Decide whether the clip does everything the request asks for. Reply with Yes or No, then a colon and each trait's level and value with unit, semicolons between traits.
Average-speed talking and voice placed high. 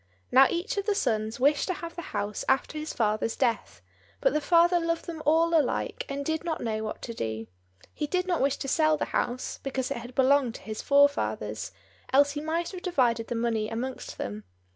No: fast, 210 wpm; very high, 280 Hz